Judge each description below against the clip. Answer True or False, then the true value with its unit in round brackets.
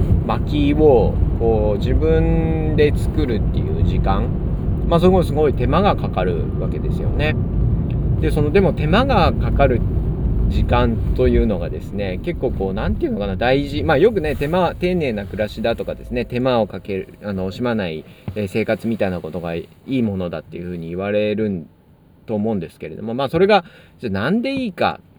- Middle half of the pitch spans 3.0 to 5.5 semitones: True (5.1 semitones)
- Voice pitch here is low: True (105 Hz)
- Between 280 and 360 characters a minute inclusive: True (355 characters per minute)